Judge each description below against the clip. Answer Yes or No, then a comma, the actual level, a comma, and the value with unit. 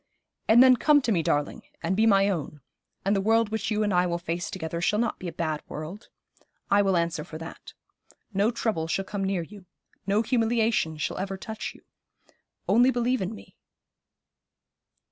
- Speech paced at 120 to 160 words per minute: No, average, 185 wpm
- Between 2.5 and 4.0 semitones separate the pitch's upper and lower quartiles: No, average, 4.6 semitones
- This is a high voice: Yes, high, 195 Hz